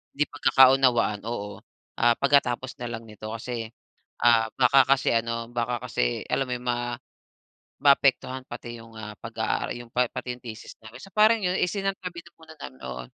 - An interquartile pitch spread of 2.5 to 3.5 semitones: Yes, average, 3.0 semitones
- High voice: No, low, 120 Hz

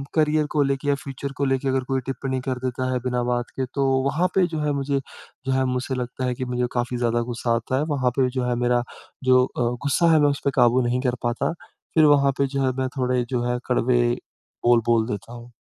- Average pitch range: No, narrow, 2.0 semitones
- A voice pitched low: Yes, low, 130 Hz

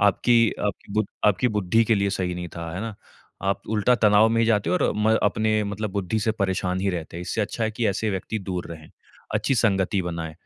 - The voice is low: Yes, low, 100 Hz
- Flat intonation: No, average, 3.0 semitones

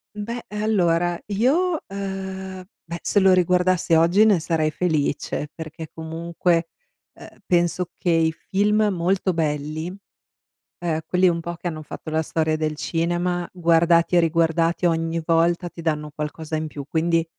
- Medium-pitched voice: Yes, medium, 170 Hz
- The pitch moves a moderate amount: No, narrow, 2.3 semitones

